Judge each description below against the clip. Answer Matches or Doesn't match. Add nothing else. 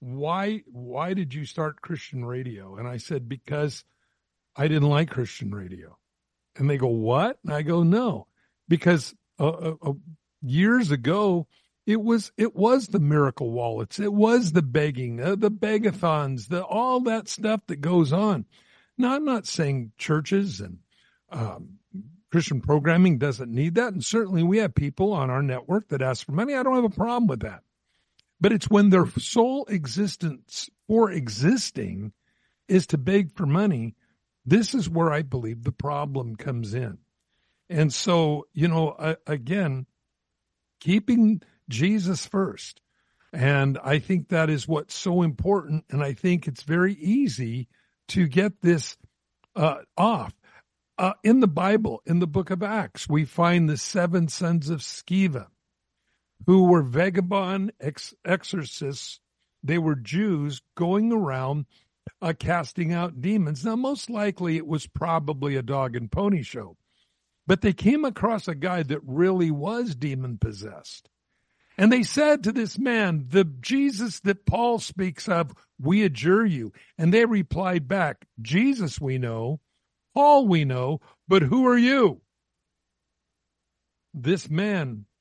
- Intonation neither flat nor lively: Doesn't match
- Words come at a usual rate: Matches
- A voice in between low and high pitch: Matches